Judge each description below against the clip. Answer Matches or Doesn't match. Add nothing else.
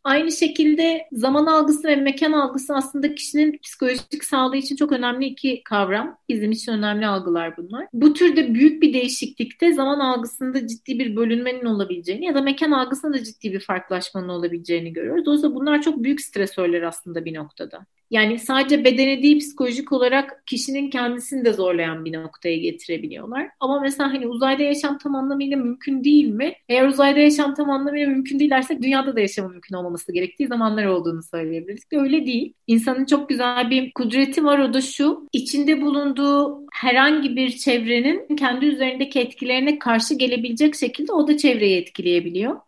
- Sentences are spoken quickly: Matches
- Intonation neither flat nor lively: Matches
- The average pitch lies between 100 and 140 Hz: Doesn't match